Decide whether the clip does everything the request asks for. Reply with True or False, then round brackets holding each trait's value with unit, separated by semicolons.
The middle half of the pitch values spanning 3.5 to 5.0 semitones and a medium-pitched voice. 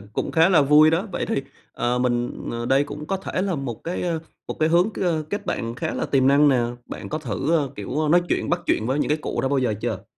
True (4.3 semitones; 150 Hz)